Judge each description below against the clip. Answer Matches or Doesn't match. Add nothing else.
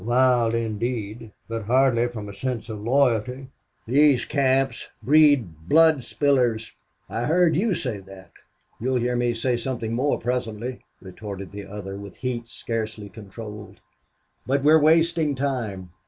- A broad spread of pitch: Doesn't match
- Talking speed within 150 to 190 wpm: Doesn't match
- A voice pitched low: Matches